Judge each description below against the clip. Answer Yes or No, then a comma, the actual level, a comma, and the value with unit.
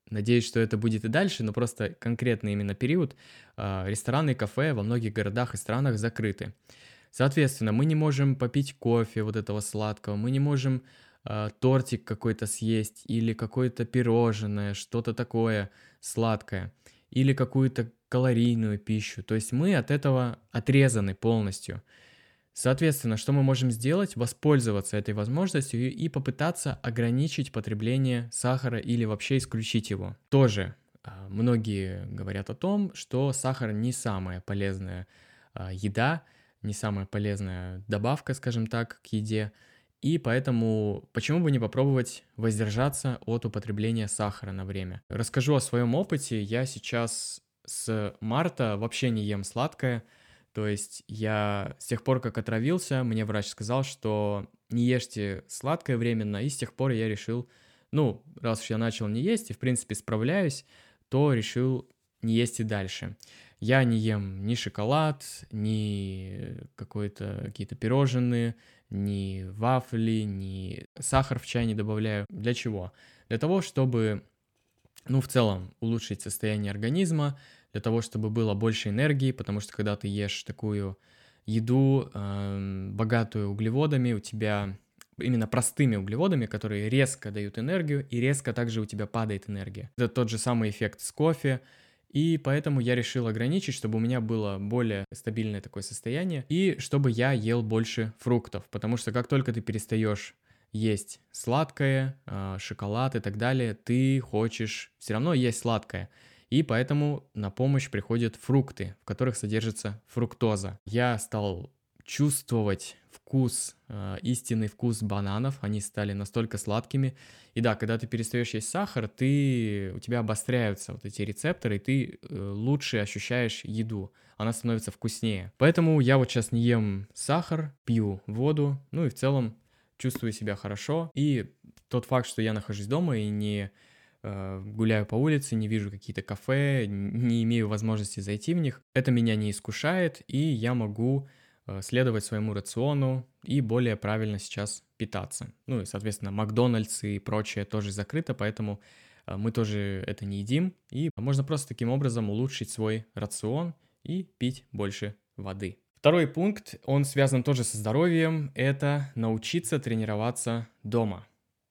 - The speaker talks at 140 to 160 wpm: Yes, average, 145 wpm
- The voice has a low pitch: Yes, low, 115 Hz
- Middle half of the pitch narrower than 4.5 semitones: Yes, average, 3.7 semitones